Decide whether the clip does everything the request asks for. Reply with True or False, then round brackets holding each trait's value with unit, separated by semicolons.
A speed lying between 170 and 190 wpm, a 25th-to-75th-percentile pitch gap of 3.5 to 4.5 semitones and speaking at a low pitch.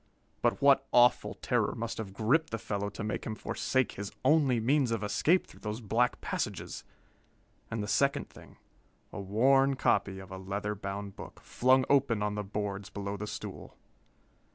True (175 wpm; 4.2 semitones; 110 Hz)